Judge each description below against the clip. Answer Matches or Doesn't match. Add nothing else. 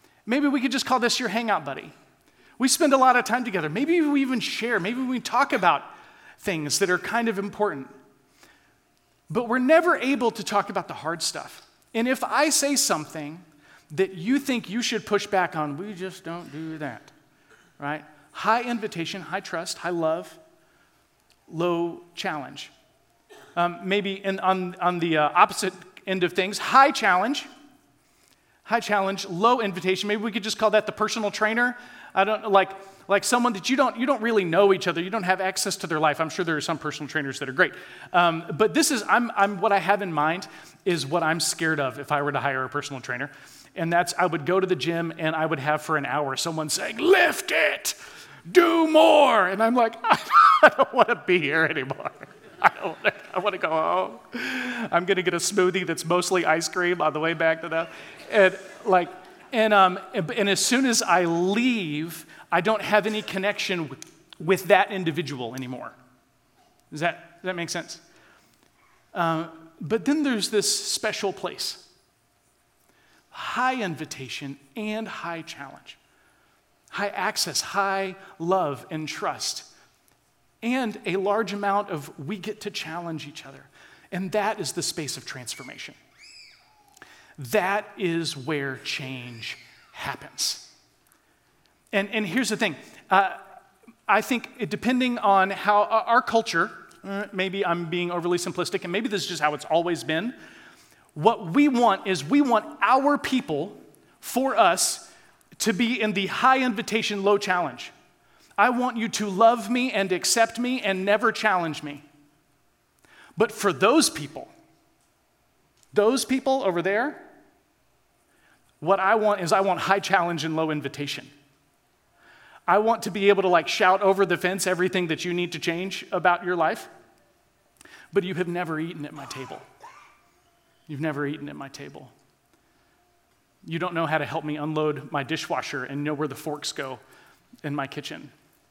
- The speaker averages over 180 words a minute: Doesn't match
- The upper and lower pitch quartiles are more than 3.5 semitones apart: Matches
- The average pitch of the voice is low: Doesn't match